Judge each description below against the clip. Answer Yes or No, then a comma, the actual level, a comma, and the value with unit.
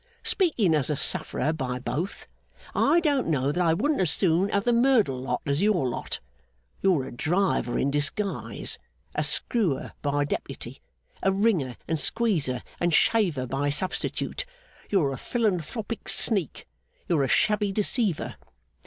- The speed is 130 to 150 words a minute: Yes, average, 145 wpm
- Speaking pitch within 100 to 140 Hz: No, medium, 175 Hz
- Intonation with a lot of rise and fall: Yes, wide, 6.9 semitones